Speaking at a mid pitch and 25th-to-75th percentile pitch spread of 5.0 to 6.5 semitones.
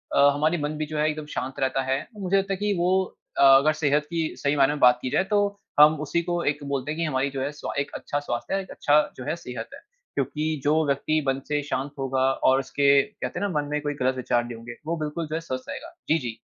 No: medium, 150 Hz; average, 2.9 semitones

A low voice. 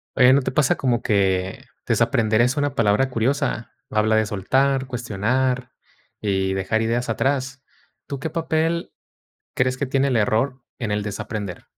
Yes: low, 120 Hz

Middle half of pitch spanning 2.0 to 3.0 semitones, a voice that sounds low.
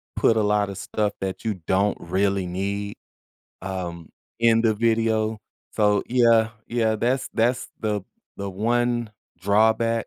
Yes: narrow, 2.5 semitones; low, 110 Hz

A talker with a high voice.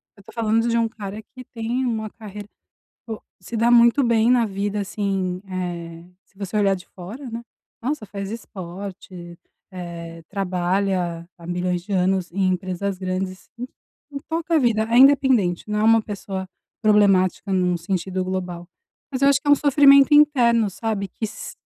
Yes: high, 200 Hz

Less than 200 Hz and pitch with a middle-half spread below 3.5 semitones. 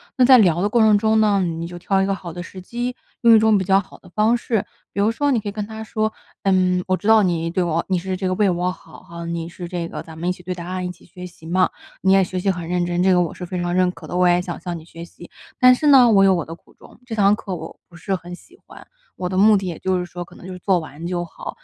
Yes: medium, 185 Hz; average, 2.8 semitones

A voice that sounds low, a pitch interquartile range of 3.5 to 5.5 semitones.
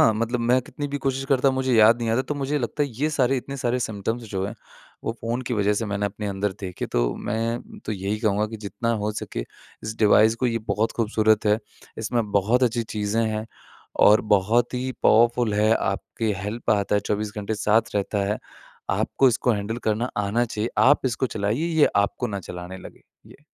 No: low, 110 Hz; average, 3.0 semitones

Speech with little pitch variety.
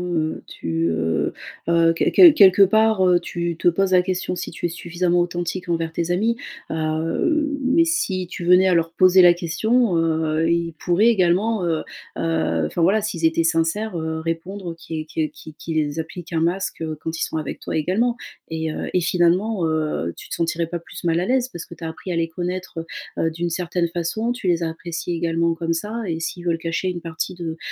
Yes: narrow, 2.3 semitones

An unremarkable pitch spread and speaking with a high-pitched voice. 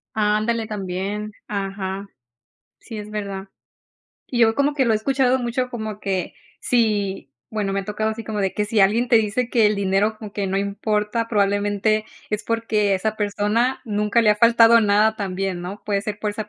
No: narrow, 1.9 semitones; high, 210 Hz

